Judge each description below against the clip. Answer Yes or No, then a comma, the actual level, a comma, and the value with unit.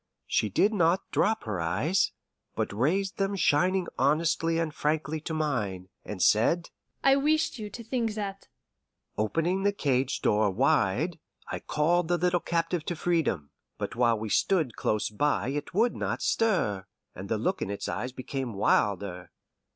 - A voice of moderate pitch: Yes, medium, 155 Hz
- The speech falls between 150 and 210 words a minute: Yes, average, 160 wpm